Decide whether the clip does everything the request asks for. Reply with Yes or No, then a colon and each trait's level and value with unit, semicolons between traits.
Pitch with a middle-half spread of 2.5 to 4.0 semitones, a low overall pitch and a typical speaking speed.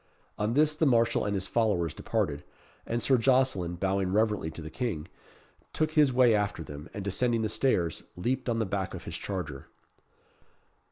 No: wide, 5.6 semitones; low, 105 Hz; average, 175 wpm